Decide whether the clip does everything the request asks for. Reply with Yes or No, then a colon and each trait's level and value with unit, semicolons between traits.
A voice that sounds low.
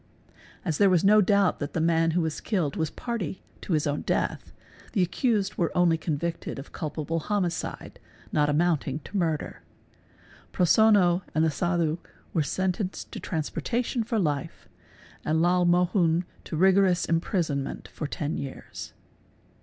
No: medium, 170 Hz